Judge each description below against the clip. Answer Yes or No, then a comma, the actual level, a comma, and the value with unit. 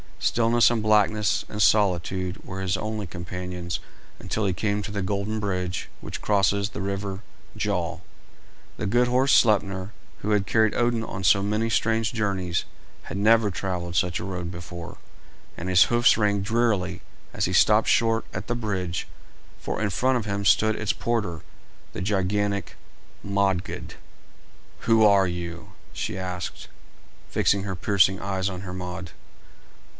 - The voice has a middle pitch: No, low, 100 Hz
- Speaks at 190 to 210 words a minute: No, average, 150 wpm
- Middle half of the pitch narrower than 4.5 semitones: Yes, average, 2.8 semitones